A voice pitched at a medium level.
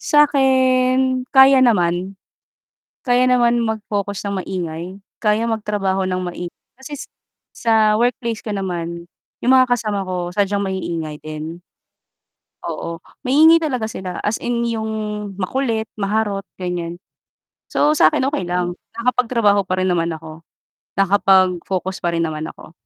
No: high, 205 Hz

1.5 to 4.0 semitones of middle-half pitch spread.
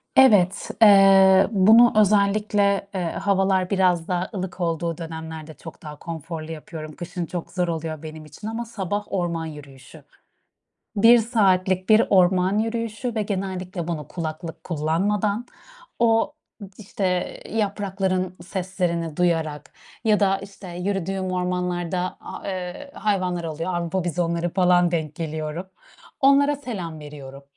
Yes: average, 3.3 semitones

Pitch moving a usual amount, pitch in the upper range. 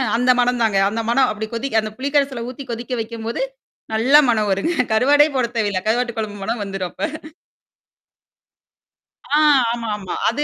Yes: average, 3.4 semitones; high, 235 Hz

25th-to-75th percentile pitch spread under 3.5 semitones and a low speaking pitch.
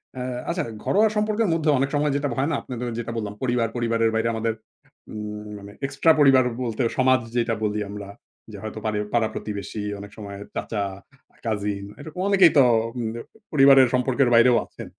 No: average, 4.3 semitones; low, 120 Hz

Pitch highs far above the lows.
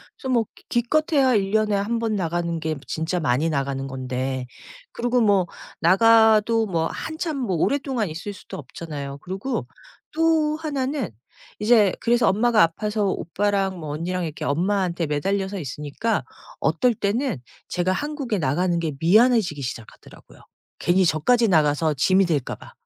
Yes: wide, 6.3 semitones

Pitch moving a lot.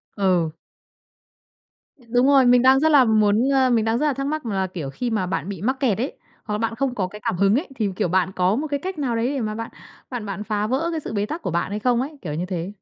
No: average, 5.0 semitones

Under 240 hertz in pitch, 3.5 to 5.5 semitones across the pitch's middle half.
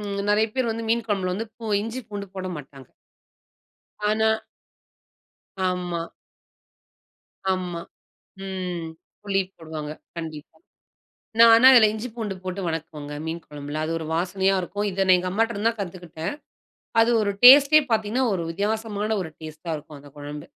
Yes: high, 190 Hz; average, 5.1 semitones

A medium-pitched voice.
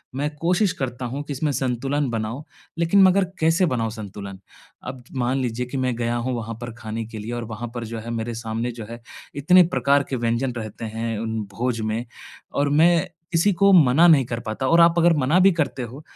No: low, 125 Hz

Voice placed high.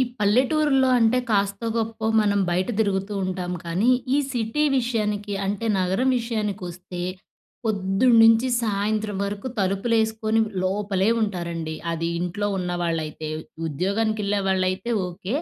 Yes: high, 205 Hz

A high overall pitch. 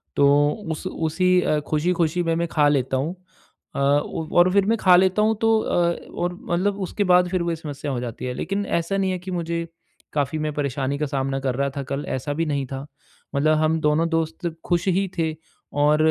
No: medium, 160 Hz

